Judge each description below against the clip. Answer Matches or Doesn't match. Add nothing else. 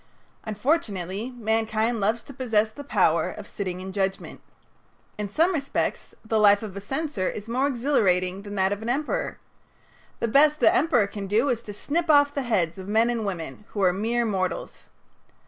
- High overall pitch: Matches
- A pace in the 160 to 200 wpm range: Matches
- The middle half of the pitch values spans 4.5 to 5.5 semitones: Matches